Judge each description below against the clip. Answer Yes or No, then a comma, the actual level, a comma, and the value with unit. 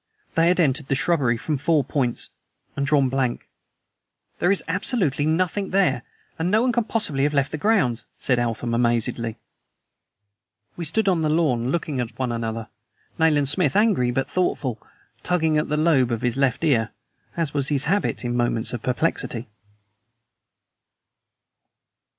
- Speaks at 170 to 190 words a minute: No, average, 155 wpm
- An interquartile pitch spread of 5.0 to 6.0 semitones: Yes, average, 5.3 semitones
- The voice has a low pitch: No, medium, 145 Hz